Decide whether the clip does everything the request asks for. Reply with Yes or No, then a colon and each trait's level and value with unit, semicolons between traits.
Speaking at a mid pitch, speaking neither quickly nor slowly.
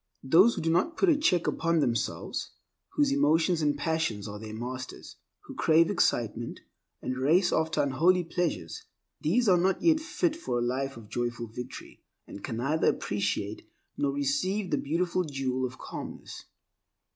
Yes: medium, 150 Hz; average, 160 wpm